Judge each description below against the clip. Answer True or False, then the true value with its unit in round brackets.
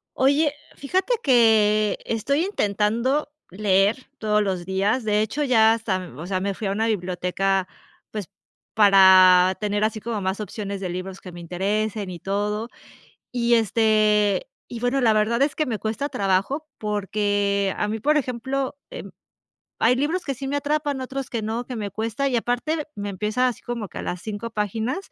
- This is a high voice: True (215 Hz)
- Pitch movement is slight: False (3.8 semitones)